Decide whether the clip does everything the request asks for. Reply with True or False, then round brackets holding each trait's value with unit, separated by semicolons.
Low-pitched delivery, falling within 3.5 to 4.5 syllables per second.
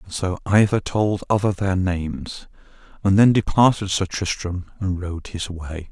True (95 Hz; 4.3 syllables/s)